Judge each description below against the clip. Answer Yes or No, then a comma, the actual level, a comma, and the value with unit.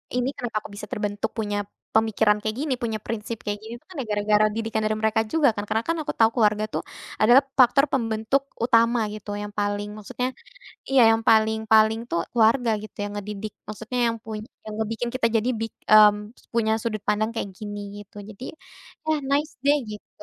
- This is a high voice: Yes, high, 220 Hz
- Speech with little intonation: Yes, narrow, 1.9 semitones